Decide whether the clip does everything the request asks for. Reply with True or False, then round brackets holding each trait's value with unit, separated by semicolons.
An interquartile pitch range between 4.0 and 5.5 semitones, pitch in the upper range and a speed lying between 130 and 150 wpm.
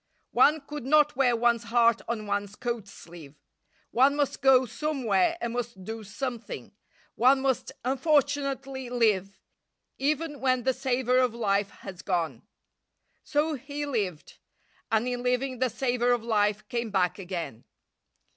True (4.3 semitones; 245 Hz; 140 wpm)